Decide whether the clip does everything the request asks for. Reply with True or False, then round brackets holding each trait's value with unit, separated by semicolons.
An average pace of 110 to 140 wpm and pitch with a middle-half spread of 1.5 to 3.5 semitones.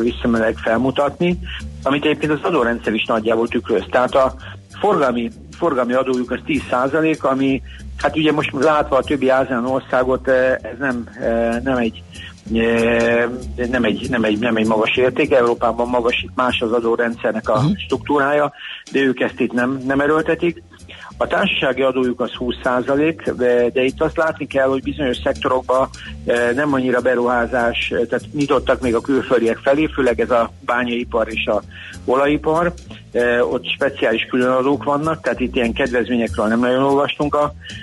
False (150 wpm; 2.8 semitones)